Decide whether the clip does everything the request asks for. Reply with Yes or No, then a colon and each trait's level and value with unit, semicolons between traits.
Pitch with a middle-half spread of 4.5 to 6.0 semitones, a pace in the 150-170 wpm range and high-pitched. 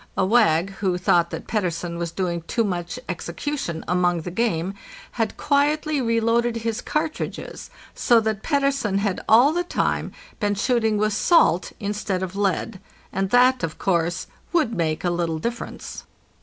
Yes: average, 5.3 semitones; average, 155 wpm; high, 205 Hz